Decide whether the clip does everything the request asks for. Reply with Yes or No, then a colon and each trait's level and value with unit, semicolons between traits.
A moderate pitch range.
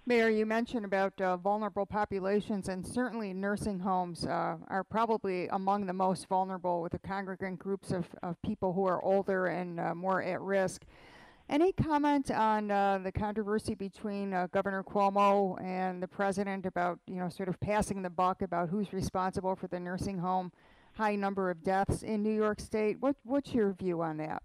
No: narrow, 2.2 semitones